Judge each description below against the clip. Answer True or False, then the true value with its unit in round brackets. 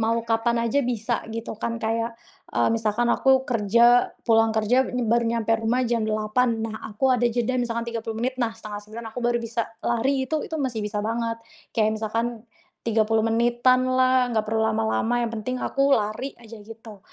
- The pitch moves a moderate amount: False (1.6 semitones)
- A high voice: True (230 Hz)